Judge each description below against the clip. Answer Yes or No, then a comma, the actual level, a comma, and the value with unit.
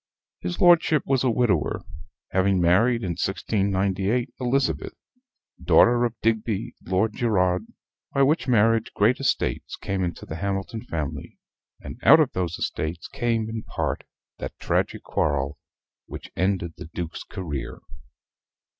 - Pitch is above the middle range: No, low, 100 Hz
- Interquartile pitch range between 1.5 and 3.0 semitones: No, average, 5.0 semitones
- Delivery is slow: Yes, slow, 130 wpm